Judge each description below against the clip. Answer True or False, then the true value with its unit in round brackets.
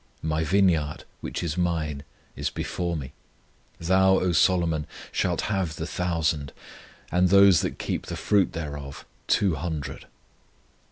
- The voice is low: True (85 Hz)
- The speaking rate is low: True (130 wpm)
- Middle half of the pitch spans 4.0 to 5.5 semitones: False (3.1 semitones)